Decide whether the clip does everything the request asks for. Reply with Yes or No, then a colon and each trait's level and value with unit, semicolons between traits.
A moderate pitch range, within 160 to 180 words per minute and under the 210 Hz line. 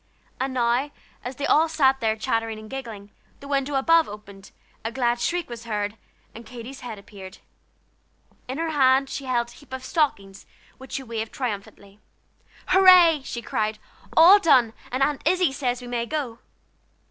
No: average, 4.0 semitones; average, 170 wpm; very high, 255 Hz